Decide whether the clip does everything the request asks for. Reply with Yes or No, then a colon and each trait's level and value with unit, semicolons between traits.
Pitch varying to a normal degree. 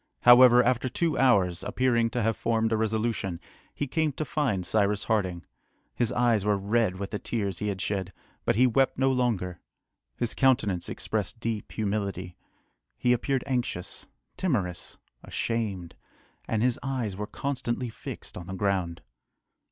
Yes: average, 4.1 semitones